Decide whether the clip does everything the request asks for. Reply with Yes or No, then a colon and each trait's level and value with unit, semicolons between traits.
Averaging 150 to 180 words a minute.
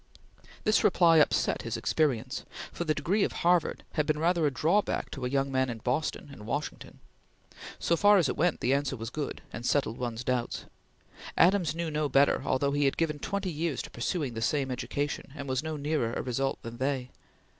No: fast, 205 wpm